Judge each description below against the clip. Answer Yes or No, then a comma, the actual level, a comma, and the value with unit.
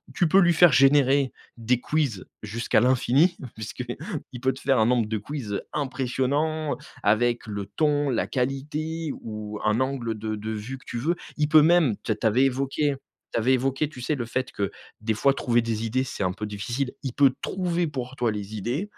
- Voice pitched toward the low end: Yes, low, 130 Hz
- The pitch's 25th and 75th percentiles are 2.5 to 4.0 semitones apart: No, average, 4.4 semitones